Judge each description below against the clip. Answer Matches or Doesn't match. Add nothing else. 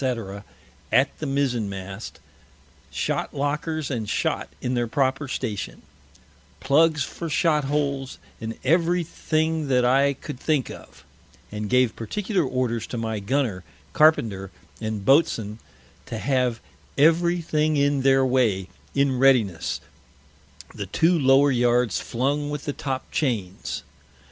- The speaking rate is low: Matches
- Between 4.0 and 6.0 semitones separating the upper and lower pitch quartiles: Matches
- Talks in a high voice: Doesn't match